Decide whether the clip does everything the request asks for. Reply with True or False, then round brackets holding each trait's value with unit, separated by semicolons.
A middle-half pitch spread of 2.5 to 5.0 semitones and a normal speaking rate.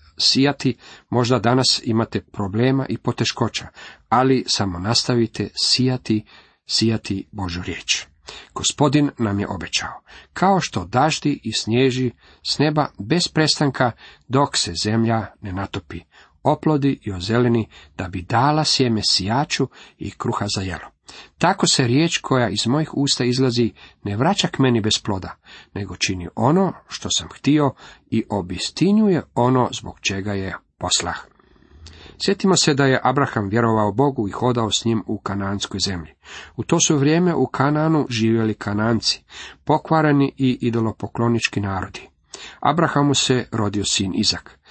False (5.5 semitones; 135 wpm)